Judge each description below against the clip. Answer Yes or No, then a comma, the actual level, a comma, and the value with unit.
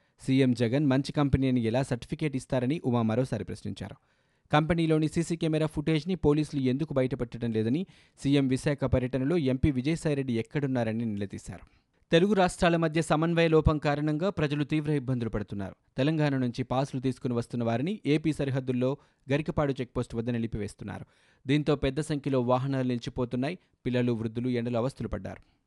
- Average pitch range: Yes, average, 4.1 semitones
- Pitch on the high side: No, low, 130 Hz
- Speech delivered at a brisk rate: Yes, fast, 130 wpm